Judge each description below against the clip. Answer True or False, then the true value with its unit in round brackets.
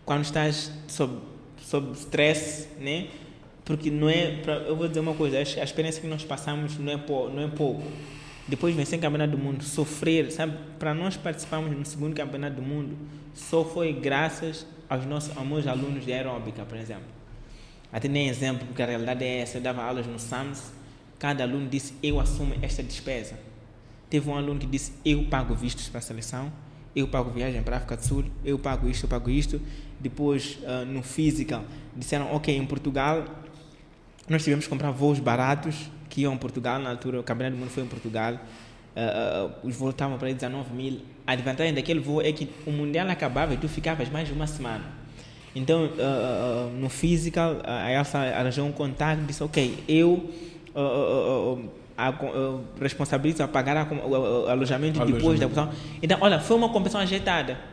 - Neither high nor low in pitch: True (145 Hz)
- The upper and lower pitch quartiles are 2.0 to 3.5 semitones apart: True (2.8 semitones)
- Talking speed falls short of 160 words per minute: False (185 wpm)